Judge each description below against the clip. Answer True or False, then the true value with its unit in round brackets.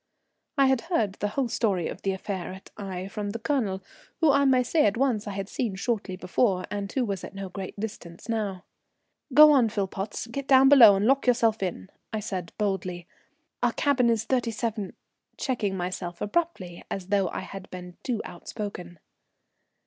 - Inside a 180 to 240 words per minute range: True (185 wpm)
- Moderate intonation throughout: True (4.4 semitones)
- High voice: True (205 Hz)